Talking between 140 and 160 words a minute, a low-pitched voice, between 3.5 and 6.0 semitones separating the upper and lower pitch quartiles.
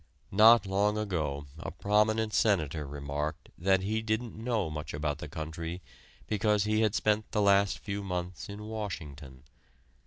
Yes: average, 150 wpm; low, 100 Hz; wide, 5.5 semitones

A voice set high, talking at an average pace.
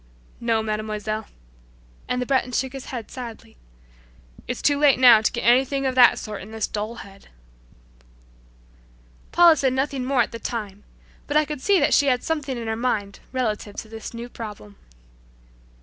Yes: high, 240 Hz; average, 175 wpm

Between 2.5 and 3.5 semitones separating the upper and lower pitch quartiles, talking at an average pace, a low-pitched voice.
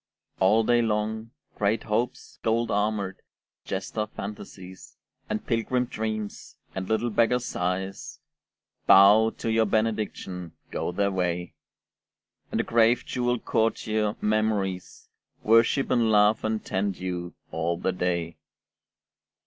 No: average, 2.9 semitones; slow, 115 wpm; low, 105 Hz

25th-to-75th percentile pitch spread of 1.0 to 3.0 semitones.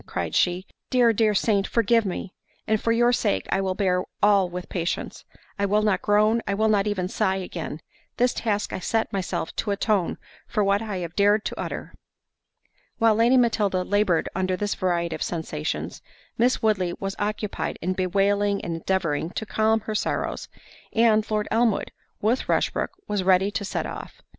Yes: average, 2.7 semitones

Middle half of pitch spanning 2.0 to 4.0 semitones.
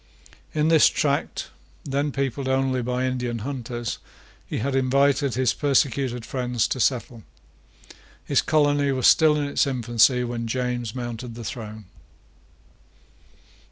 Yes: average, 2.7 semitones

